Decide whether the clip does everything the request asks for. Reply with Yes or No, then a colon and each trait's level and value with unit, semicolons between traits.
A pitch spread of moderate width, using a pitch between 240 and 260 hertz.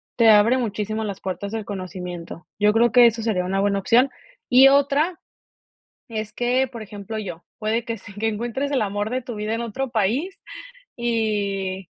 No: average, 3.0 semitones; high, 220 Hz